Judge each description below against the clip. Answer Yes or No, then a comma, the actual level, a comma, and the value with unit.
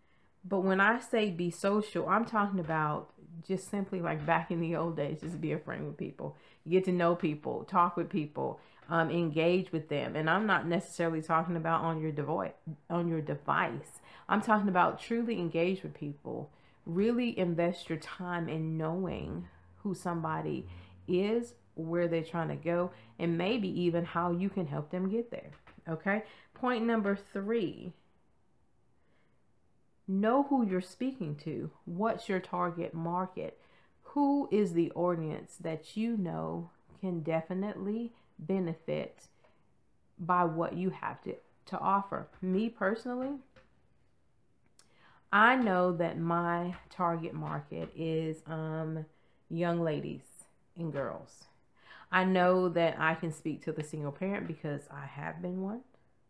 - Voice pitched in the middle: Yes, medium, 175 Hz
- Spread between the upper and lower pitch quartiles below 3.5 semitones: Yes, average, 3.1 semitones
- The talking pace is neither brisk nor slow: Yes, average, 145 wpm